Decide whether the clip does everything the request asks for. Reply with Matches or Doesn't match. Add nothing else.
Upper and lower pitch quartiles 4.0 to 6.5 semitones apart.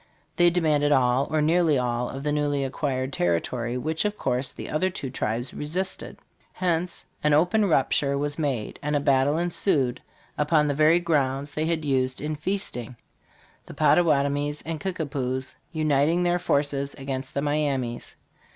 Doesn't match